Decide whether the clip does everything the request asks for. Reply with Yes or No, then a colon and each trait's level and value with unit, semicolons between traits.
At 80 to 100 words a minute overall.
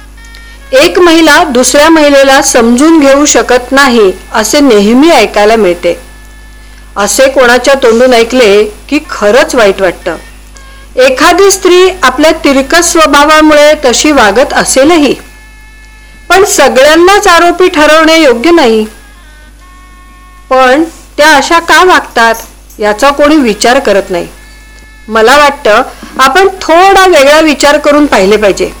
No: average, 110 wpm